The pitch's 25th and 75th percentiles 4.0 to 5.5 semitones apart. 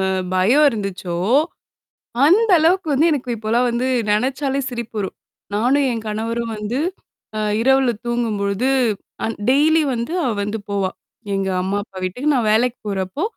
Yes: average, 4.6 semitones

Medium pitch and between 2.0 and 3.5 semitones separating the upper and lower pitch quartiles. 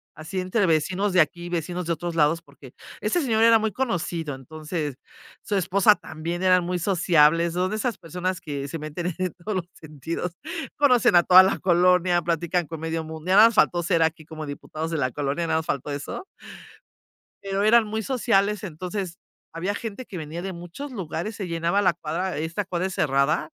Yes: medium, 175 Hz; average, 3.2 semitones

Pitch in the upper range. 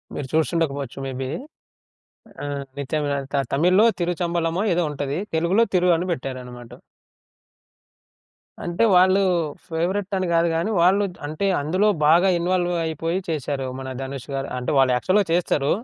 No: medium, 165 Hz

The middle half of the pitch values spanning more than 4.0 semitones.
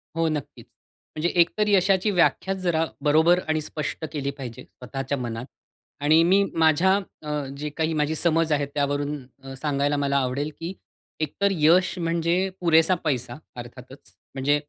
No: average, 3.1 semitones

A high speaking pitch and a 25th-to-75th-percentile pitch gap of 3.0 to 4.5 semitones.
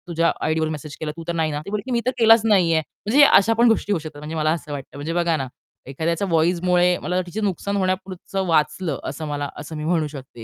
No: medium, 170 Hz; average, 3.6 semitones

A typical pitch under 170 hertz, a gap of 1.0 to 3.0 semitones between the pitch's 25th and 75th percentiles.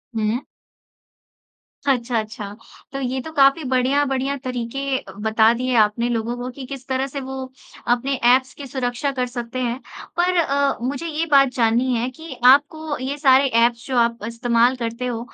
No: very high, 255 Hz; narrow, 2.6 semitones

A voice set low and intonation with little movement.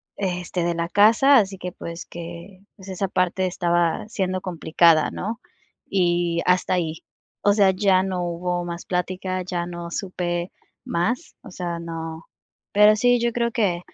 No: medium, 180 Hz; narrow, 2.2 semitones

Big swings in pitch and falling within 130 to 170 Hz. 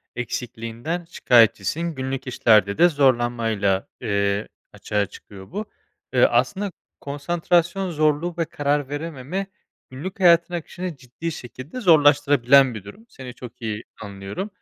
Yes: wide, 6.5 semitones; medium, 140 Hz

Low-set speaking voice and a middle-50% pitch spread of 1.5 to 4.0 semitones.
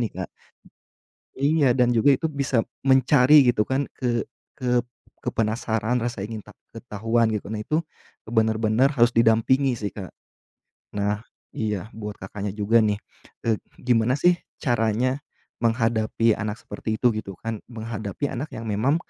Yes: low, 115 Hz; average, 2.7 semitones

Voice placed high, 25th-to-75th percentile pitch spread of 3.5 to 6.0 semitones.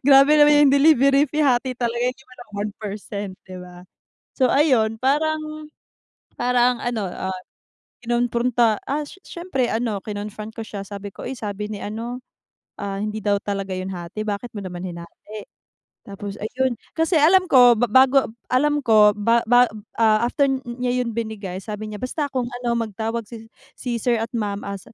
Yes: high, 230 Hz; average, 4.1 semitones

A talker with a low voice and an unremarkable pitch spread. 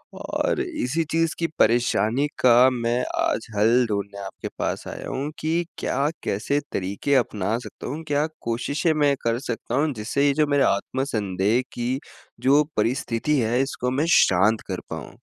Yes: low, 125 Hz; average, 4.3 semitones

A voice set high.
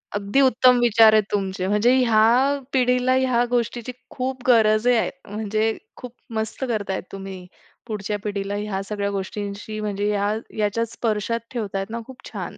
Yes: high, 215 Hz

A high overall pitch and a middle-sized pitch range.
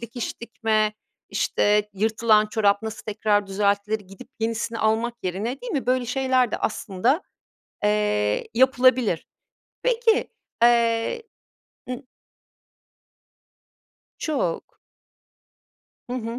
Yes: high, 225 Hz; average, 3.1 semitones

